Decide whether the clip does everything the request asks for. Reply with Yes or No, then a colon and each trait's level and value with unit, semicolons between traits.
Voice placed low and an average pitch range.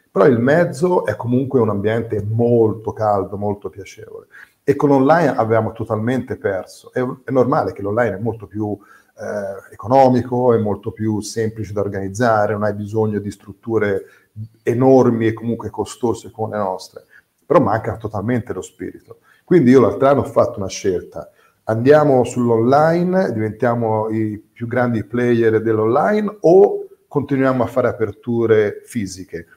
Yes: low, 115 Hz; average, 3.1 semitones